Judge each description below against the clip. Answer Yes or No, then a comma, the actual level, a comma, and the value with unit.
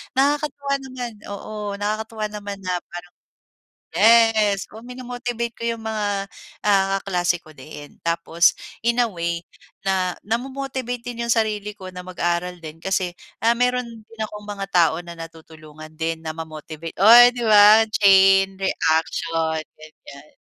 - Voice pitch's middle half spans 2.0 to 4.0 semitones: No, average, 5.3 semitones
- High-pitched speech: Yes, high, 200 Hz